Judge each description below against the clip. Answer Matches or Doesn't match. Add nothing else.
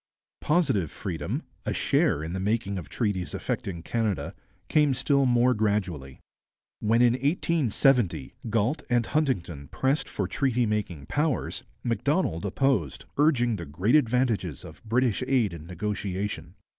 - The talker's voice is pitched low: Matches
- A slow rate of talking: Matches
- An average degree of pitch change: Doesn't match